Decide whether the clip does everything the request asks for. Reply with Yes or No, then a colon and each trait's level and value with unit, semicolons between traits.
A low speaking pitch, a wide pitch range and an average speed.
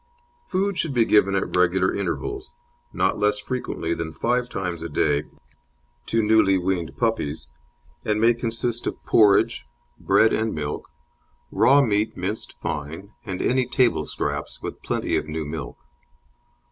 Yes: low, 105 Hz; wide, 5.8 semitones; average, 145 wpm